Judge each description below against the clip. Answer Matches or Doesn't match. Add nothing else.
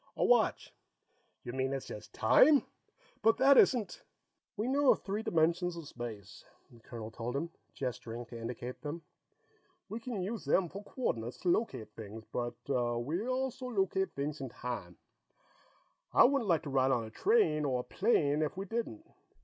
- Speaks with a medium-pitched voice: Matches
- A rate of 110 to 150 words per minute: Doesn't match